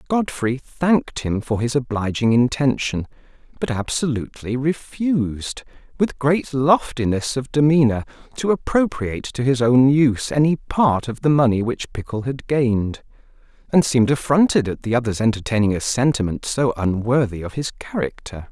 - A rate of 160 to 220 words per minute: No, average, 145 wpm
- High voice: No, low, 130 Hz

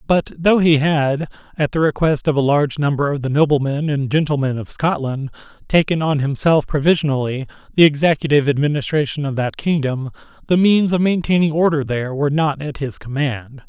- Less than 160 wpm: No, average, 170 wpm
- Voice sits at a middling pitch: Yes, medium, 145 Hz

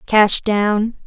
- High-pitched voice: Yes, high, 210 Hz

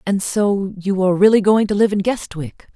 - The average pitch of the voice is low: No, high, 200 Hz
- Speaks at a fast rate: Yes, fast, 220 wpm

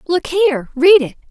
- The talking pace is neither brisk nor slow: Yes, average, 185 wpm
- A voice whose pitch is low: No, very high, 325 Hz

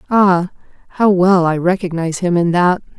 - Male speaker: No, female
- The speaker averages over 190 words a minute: No, average, 160 wpm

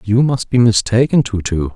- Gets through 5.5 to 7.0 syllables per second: No, 4.9 syllables/s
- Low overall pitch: Yes, low, 110 Hz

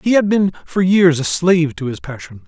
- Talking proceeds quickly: Yes, fast, 245 wpm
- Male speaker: Yes, male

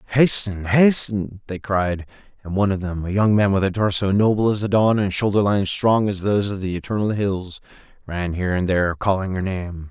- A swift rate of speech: Yes, fast, 210 wpm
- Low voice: Yes, low, 100 Hz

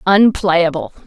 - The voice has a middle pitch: Yes, medium, 175 Hz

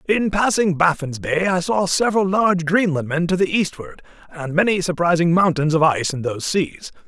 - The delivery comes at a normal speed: Yes, average, 180 wpm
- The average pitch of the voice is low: No, medium, 175 Hz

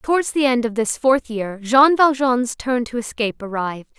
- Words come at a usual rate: Yes, average, 195 wpm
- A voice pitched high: Yes, high, 245 Hz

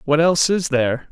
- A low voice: No, medium, 150 Hz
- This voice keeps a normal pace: No, fast, 215 wpm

